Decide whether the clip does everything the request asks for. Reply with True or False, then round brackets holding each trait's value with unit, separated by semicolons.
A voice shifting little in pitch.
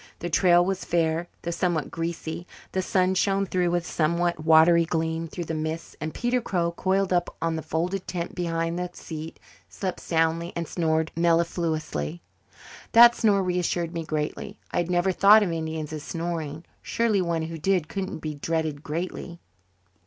True (2.1 semitones)